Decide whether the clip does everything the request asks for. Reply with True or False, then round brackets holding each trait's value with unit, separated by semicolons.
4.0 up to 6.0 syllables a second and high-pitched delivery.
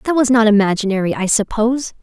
False (6.5 syllables/s; 225 Hz)